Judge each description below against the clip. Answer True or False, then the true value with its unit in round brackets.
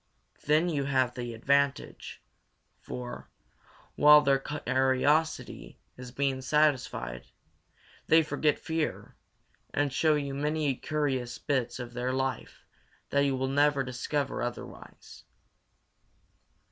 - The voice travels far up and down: False (2.7 semitones)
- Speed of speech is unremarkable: False (110 wpm)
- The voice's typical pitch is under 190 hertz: True (135 Hz)